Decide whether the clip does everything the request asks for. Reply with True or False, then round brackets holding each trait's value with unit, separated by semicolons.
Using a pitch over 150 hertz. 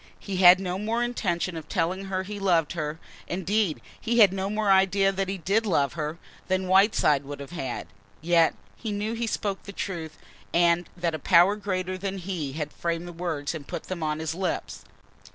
True (185 Hz)